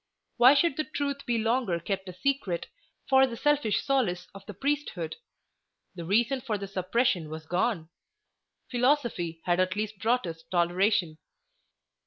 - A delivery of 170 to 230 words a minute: No, average, 150 wpm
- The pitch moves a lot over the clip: Yes, wide, 6.7 semitones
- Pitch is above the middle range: Yes, high, 210 Hz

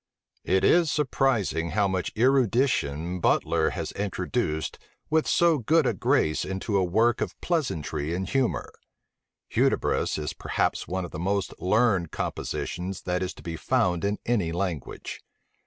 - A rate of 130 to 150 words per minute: Yes, average, 145 wpm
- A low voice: Yes, very low, 95 Hz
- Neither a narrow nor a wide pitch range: No, wide, 5.7 semitones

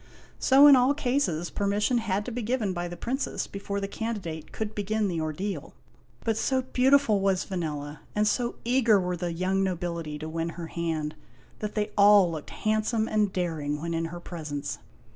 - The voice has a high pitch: Yes, high, 195 Hz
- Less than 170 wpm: No, average, 185 wpm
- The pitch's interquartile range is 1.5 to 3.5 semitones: No, average, 4.7 semitones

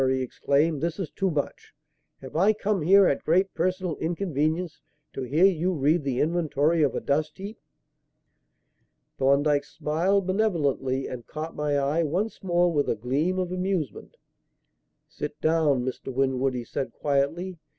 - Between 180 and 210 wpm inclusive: No, average, 150 wpm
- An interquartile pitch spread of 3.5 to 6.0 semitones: Yes, average, 4.5 semitones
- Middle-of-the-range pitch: Yes, medium, 155 Hz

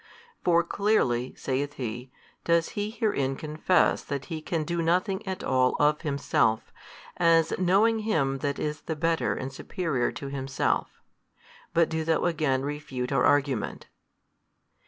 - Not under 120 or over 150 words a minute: Yes, average, 140 wpm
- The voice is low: No, medium, 150 Hz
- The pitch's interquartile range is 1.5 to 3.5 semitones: No, average, 4.1 semitones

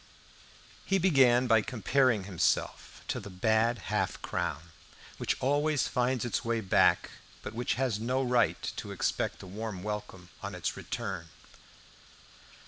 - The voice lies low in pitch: Yes, low, 115 Hz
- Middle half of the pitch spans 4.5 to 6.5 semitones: No, average, 4.0 semitones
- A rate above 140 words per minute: No, slow, 135 wpm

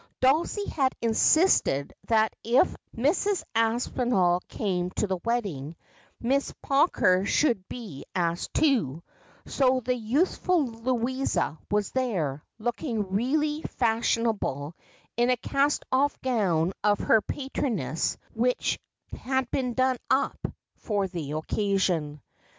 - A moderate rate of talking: No, slow, 115 wpm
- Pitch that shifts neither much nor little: No, wide, 5.9 semitones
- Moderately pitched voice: No, high, 230 Hz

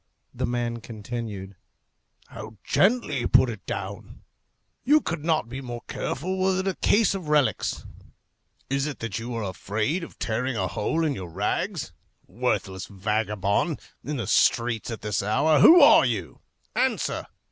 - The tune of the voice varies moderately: No, wide, 6.7 semitones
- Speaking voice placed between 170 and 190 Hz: No, low, 120 Hz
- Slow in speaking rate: No, average, 160 wpm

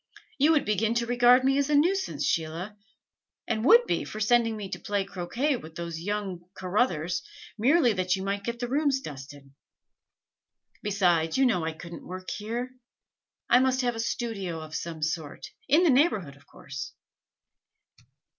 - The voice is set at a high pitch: Yes, high, 210 Hz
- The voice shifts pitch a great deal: Yes, wide, 6.5 semitones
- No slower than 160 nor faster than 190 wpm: Yes, average, 165 wpm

